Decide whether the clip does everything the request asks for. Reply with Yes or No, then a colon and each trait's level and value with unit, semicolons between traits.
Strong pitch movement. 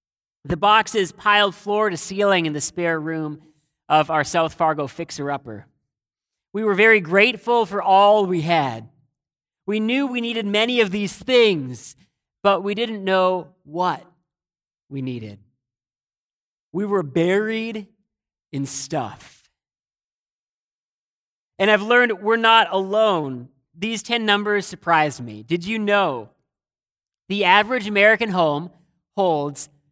Yes: wide, 5.8 semitones